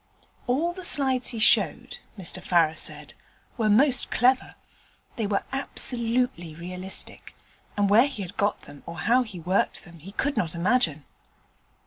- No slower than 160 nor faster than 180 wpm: No, average, 150 wpm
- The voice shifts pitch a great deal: Yes, wide, 6.6 semitones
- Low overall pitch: No, high, 205 Hz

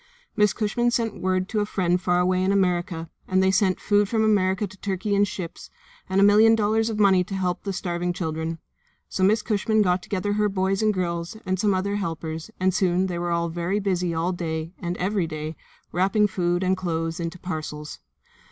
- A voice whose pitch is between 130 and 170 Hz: No, medium, 185 Hz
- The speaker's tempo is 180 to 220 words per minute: Yes, average, 200 wpm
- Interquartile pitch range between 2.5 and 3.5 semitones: Yes, average, 2.8 semitones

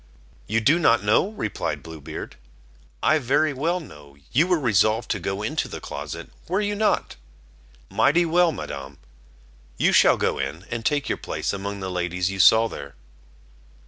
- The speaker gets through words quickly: No, average, 170 wpm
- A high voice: No, low, 115 Hz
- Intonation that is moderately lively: No, wide, 8.8 semitones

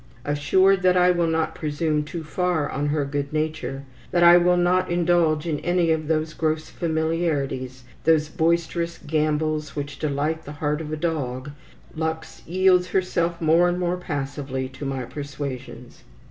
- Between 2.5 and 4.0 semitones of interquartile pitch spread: Yes, average, 2.9 semitones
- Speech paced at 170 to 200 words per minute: No, average, 160 wpm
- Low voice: No, medium, 155 Hz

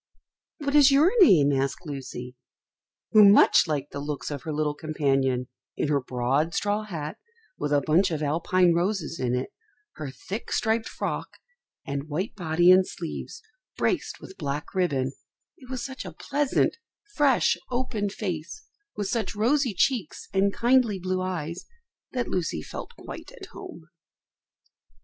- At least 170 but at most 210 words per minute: No, average, 150 wpm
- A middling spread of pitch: No, wide, 6.8 semitones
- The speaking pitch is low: No, medium, 175 Hz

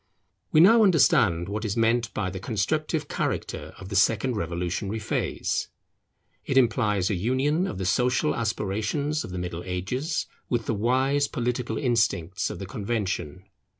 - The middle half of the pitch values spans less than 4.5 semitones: No, average, 5.2 semitones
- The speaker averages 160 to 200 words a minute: No, average, 150 wpm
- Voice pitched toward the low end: Yes, low, 110 Hz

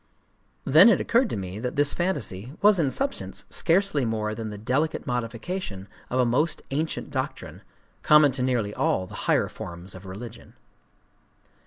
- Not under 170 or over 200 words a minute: No, average, 160 wpm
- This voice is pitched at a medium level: No, low, 125 Hz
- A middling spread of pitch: No, wide, 6.8 semitones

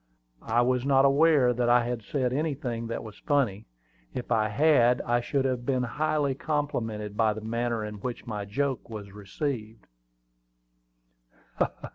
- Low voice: Yes, low, 120 Hz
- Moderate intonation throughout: Yes, average, 3.8 semitones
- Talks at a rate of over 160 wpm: No, average, 150 wpm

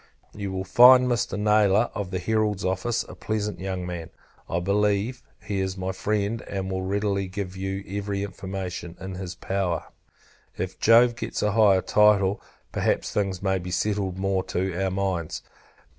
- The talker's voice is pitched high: No, very low, 95 Hz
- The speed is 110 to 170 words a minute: Yes, average, 160 wpm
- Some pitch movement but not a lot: No, narrow, 1.9 semitones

